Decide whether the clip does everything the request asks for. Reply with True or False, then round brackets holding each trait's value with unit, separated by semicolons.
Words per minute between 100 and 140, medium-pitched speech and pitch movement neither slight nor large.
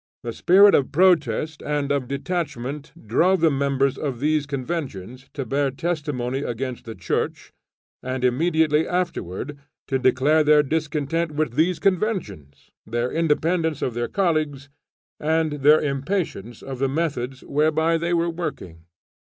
True (135 wpm; 145 Hz; 3.9 semitones)